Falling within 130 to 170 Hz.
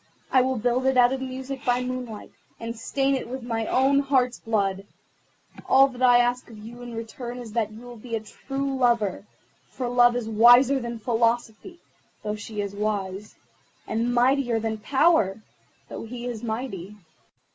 No: high, 240 Hz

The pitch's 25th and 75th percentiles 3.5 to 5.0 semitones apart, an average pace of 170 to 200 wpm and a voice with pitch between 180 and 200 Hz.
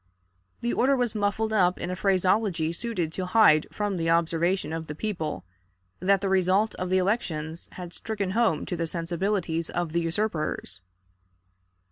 No: average, 3.8 semitones; average, 160 wpm; medium, 185 Hz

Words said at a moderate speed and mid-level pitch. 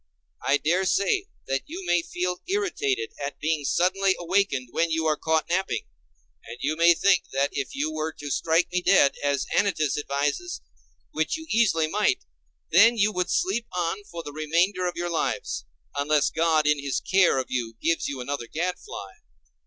Yes: average, 175 wpm; medium, 165 Hz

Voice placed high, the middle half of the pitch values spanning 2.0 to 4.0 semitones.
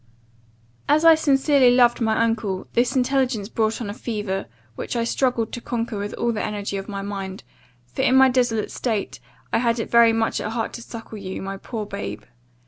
Yes: high, 225 Hz; average, 3.2 semitones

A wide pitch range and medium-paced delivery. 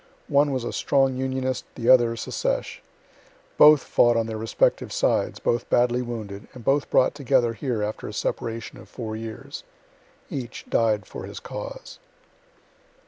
No: average, 2.7 semitones; average, 150 wpm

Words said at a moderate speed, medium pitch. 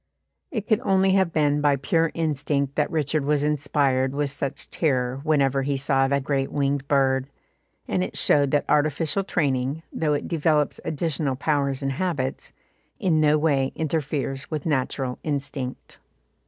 Yes: average, 155 wpm; medium, 145 Hz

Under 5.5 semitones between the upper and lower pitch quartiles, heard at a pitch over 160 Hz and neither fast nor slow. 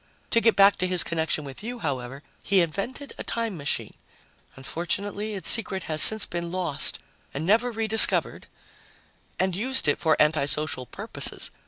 No: wide, 5.8 semitones; medium, 185 Hz; average, 165 wpm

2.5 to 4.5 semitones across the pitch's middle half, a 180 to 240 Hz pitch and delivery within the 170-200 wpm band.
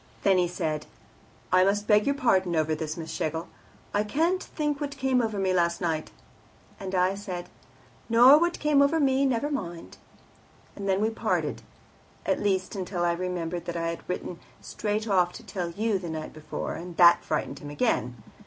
No: average, 5.1 semitones; high, 190 Hz; average, 180 wpm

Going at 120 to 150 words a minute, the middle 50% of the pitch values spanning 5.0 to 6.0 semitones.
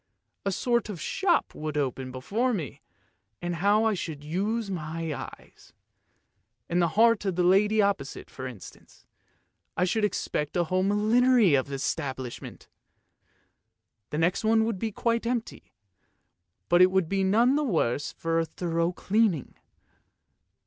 Yes: average, 140 wpm; wide, 5.6 semitones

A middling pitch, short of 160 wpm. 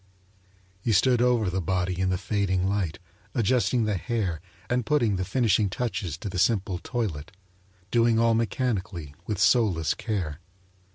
No: low, 100 Hz; average, 150 wpm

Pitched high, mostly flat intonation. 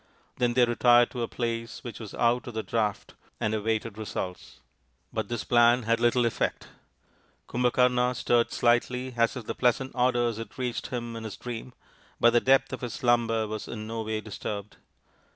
No: low, 120 Hz; narrow, 1.6 semitones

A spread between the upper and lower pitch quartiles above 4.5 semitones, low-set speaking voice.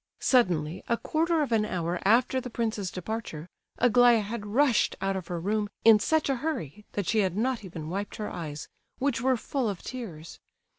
No: average, 5.1 semitones; high, 215 Hz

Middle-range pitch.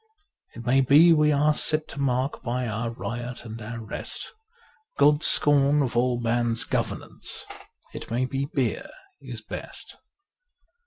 No: low, 125 Hz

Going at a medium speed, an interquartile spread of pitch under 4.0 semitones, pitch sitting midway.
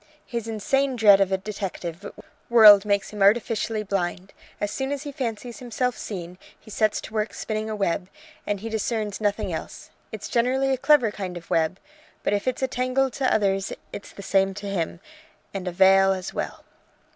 No: average, 190 wpm; average, 3.5 semitones; high, 210 Hz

